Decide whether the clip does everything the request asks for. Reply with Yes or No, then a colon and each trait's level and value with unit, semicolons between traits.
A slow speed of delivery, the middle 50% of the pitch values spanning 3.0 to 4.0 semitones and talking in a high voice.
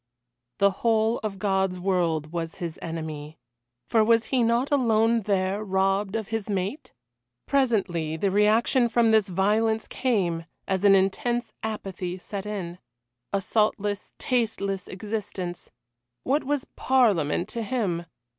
Yes: slow, 130 wpm; average, 3.4 semitones; high, 205 Hz